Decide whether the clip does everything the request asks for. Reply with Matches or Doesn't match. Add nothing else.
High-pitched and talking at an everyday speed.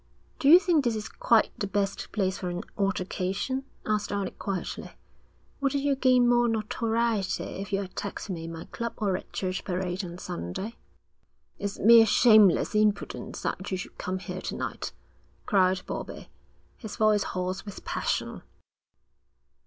Matches